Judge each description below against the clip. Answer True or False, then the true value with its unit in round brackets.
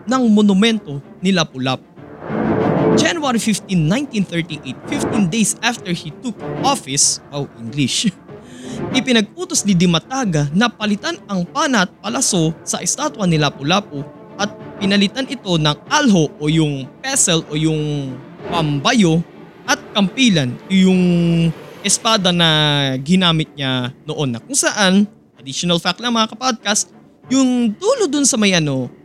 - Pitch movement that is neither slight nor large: False (6.6 semitones)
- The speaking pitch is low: False (185 Hz)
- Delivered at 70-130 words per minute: True (125 wpm)